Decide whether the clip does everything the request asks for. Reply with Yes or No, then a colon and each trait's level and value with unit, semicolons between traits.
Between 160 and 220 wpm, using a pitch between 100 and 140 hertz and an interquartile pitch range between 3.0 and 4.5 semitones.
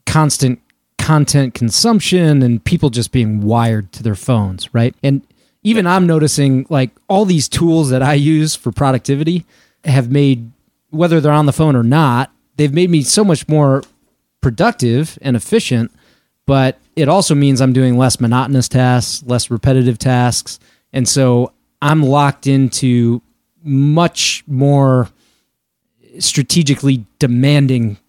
No: slow, 135 wpm; low, 135 Hz; average, 3.7 semitones